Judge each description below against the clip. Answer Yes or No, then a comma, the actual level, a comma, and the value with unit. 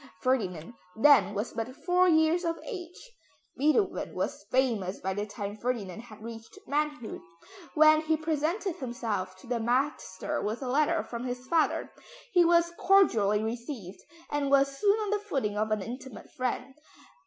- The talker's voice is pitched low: No, very high, 255 Hz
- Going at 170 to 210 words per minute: No, average, 155 wpm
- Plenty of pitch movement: Yes, wide, 6.4 semitones